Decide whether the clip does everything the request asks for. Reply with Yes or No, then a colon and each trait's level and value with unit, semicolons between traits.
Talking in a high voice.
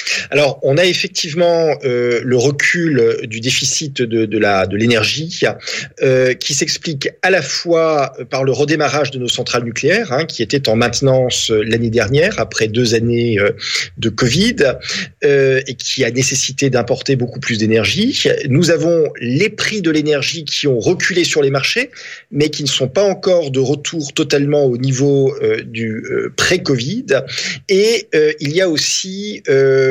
No: low, 135 Hz